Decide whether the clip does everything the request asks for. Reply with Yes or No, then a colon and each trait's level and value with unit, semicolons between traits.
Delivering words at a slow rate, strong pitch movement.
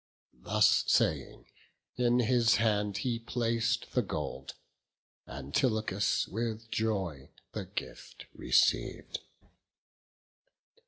No: slow, 85 wpm; average, 3.5 semitones